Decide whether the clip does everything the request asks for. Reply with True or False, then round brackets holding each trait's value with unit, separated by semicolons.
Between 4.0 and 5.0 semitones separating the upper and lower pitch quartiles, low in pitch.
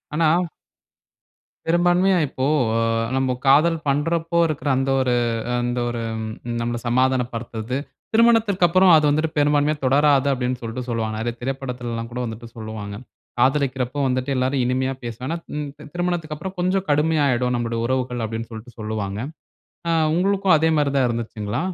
True (4.7 semitones; 130 Hz)